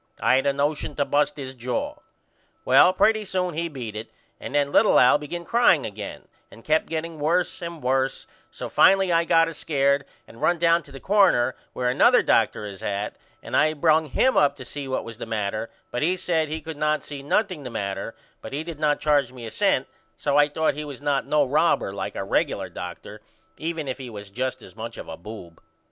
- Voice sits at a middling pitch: Yes, medium, 145 Hz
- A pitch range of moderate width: Yes, average, 4.7 semitones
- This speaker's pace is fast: Yes, fast, 220 wpm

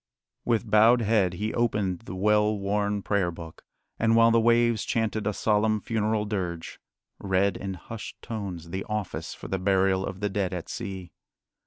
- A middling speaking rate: Yes, average, 170 wpm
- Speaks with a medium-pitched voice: No, low, 105 Hz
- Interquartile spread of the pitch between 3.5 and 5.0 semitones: No, narrow, 2.6 semitones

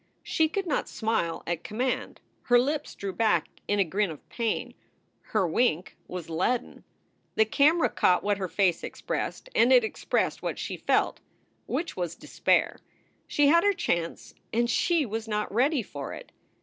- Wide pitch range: Yes, wide, 6.3 semitones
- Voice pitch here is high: Yes, high, 220 Hz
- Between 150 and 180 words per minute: Yes, average, 165 wpm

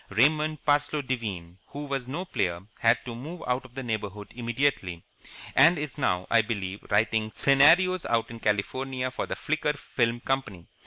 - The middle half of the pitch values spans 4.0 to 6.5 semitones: Yes, average, 5.0 semitones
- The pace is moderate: Yes, average, 165 wpm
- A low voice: Yes, low, 125 Hz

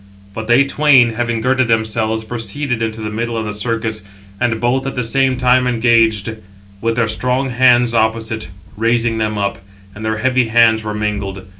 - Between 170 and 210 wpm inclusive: Yes, average, 175 wpm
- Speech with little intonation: Yes, narrow, 2.0 semitones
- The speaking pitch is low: Yes, low, 115 Hz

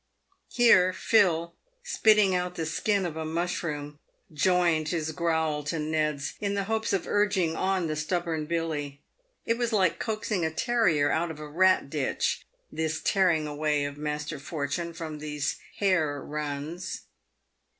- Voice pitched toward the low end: No, medium, 160 Hz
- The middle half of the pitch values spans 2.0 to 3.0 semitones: No, average, 3.6 semitones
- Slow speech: No, average, 150 wpm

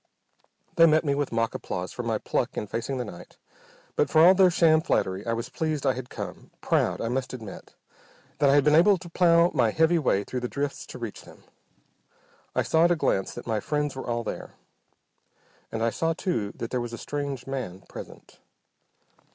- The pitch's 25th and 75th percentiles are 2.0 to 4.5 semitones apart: No, wide, 5.6 semitones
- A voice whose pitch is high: No, low, 135 Hz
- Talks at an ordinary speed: No, fast, 210 wpm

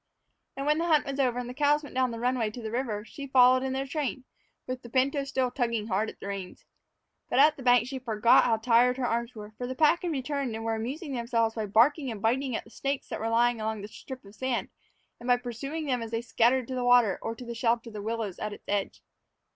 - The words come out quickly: Yes, fast, 260 wpm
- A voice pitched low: No, high, 245 Hz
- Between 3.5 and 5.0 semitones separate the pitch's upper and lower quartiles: No, average, 2.8 semitones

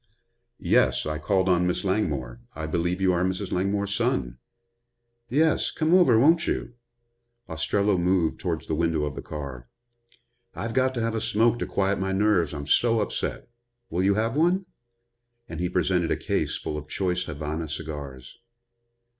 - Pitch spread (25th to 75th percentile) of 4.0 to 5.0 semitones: No, wide, 5.5 semitones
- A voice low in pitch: Yes, very low, 90 Hz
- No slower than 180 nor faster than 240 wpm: No, average, 165 wpm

